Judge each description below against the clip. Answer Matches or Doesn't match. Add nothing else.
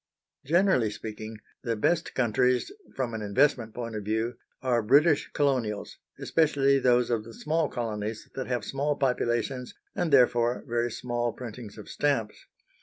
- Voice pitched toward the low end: Matches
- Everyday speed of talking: Matches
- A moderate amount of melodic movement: Matches